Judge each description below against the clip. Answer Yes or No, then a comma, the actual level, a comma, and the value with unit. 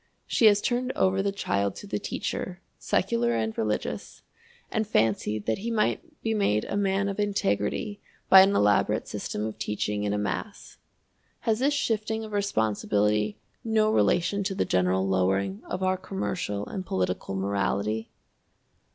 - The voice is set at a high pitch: No, low, 120 Hz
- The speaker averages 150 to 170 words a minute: Yes, average, 155 wpm